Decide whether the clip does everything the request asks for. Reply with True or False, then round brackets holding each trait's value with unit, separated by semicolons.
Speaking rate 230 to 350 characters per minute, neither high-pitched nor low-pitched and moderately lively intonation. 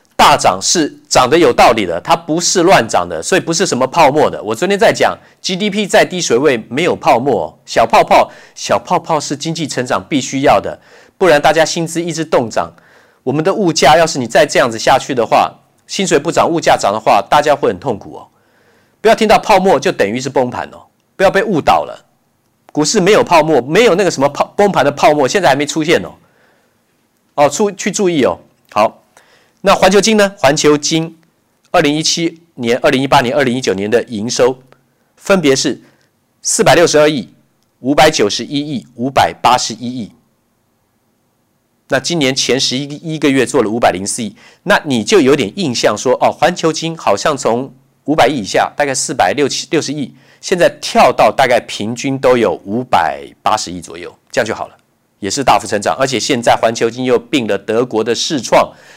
True (285 characters per minute; 150 Hz; 4.6 semitones)